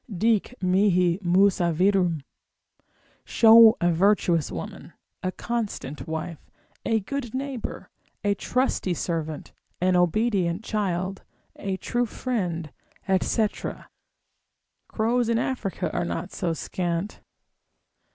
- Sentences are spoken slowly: Yes, slow, 100 wpm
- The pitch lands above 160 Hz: Yes, high, 190 Hz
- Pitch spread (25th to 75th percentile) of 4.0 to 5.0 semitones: Yes, average, 4.4 semitones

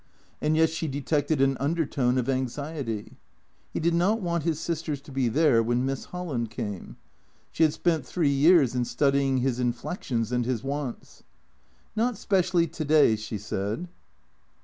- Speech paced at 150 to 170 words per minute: Yes, average, 165 wpm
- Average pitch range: Yes, average, 4.8 semitones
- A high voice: No, medium, 140 Hz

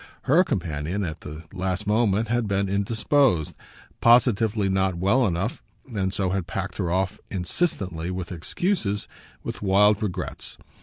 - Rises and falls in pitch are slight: No, average, 3.2 semitones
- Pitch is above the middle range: No, low, 100 Hz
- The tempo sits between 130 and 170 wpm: Yes, average, 140 wpm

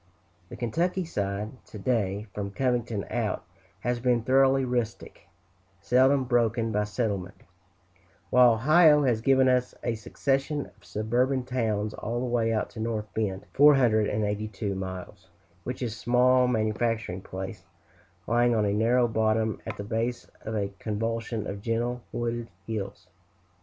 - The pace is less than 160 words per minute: Yes, average, 140 wpm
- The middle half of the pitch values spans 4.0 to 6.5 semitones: No, average, 2.8 semitones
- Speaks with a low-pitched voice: Yes, low, 115 Hz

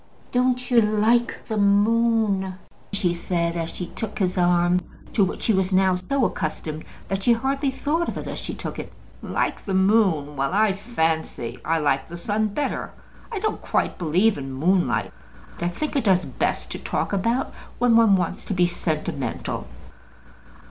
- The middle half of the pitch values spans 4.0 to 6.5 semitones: Yes, average, 4.9 semitones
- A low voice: No, high, 190 Hz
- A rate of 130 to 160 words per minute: No, average, 175 wpm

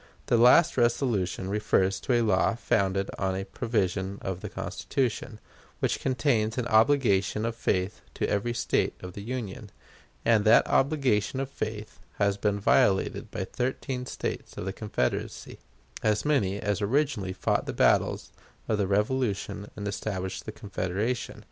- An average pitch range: Yes, average, 3.6 semitones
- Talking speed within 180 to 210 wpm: No, average, 150 wpm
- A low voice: Yes, low, 105 Hz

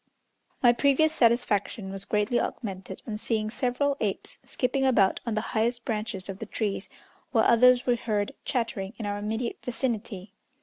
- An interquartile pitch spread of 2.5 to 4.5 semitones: Yes, average, 3.1 semitones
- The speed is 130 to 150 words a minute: No, average, 160 wpm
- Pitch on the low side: No, high, 225 Hz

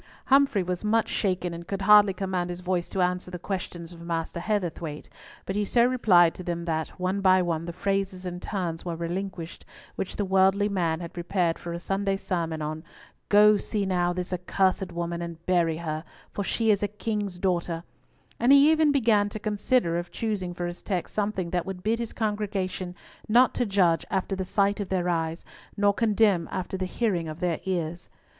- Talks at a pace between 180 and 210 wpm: Yes, average, 195 wpm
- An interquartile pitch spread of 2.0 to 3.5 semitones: Yes, average, 3.0 semitones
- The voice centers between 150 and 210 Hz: Yes, medium, 185 Hz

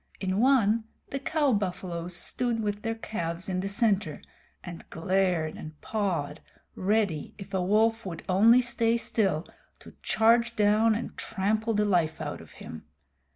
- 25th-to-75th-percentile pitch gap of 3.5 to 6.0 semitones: Yes, average, 3.8 semitones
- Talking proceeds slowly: No, average, 155 wpm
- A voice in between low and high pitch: No, high, 205 Hz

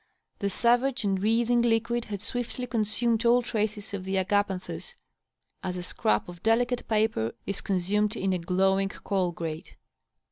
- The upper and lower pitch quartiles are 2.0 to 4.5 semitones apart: Yes, average, 3.7 semitones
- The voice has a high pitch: Yes, high, 210 Hz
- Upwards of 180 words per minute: No, average, 150 wpm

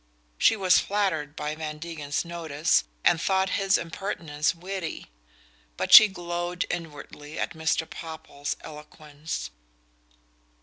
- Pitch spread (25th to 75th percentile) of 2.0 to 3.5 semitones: Yes, average, 3.0 semitones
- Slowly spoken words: Yes, slow, 115 wpm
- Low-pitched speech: No, medium, 165 Hz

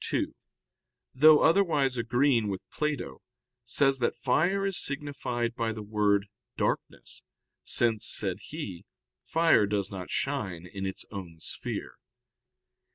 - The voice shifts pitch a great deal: Yes, wide, 6.1 semitones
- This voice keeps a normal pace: No, slow, 120 wpm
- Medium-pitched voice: No, low, 120 Hz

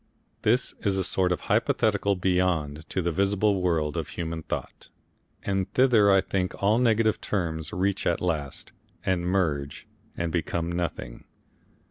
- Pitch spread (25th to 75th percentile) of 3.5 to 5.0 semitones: No, average, 3.0 semitones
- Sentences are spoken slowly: No, average, 145 wpm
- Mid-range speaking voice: No, very low, 90 Hz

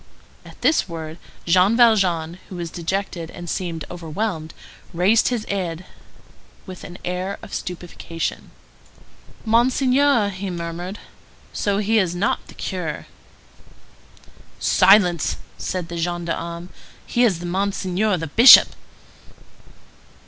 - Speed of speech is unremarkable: No, slow, 110 wpm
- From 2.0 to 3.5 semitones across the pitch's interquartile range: Yes, average, 3.1 semitones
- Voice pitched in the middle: Yes, medium, 180 Hz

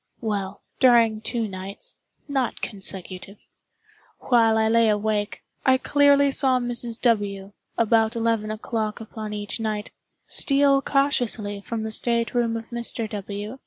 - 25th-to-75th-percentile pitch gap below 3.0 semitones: Yes, narrow, 2.5 semitones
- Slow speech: Yes, slow, 130 wpm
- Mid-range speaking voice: No, high, 225 Hz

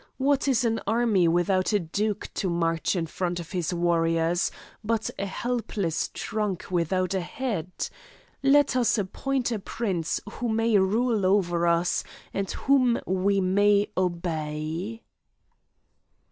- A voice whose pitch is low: No, high, 195 Hz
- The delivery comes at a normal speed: No, slow, 130 wpm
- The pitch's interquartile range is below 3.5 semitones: No, average, 4.6 semitones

